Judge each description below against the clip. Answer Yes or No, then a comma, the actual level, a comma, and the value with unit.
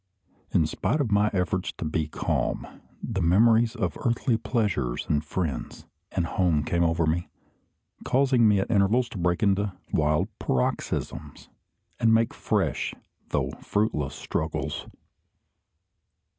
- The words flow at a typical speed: No, slow, 130 wpm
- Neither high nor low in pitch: No, very low, 95 Hz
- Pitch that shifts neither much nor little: No, wide, 5.7 semitones